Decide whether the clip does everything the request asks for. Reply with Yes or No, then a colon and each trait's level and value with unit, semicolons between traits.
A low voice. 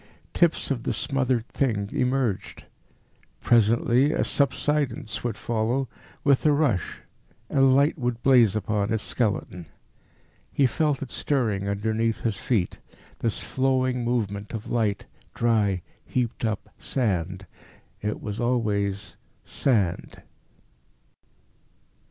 Yes: low, 115 Hz